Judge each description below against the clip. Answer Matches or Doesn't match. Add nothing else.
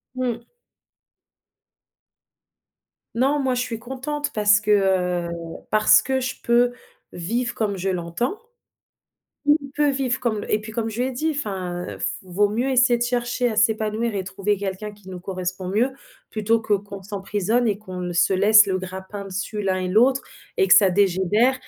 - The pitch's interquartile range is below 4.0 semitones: Doesn't match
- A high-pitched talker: Matches